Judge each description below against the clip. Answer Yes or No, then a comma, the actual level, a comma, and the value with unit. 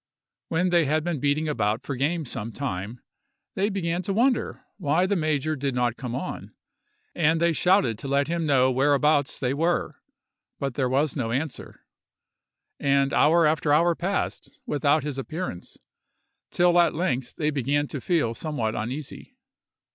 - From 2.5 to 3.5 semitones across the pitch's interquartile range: No, average, 4.1 semitones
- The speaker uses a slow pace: No, average, 160 wpm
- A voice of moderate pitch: Yes, medium, 145 Hz